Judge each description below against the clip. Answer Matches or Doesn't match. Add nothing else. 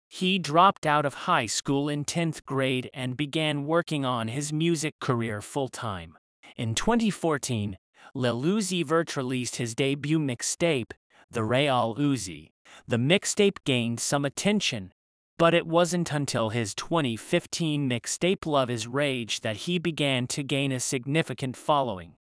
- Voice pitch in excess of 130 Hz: Matches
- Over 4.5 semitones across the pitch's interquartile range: Matches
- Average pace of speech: Matches